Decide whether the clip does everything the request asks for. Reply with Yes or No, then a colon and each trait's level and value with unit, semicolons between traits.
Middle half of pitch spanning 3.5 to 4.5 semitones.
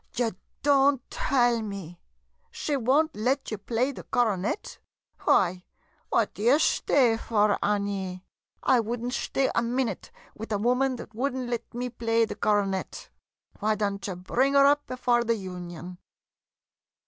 Yes: average, 3.9 semitones